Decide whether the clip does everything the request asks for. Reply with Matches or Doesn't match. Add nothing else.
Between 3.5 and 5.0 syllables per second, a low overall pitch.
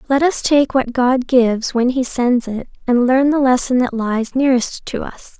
Doesn't match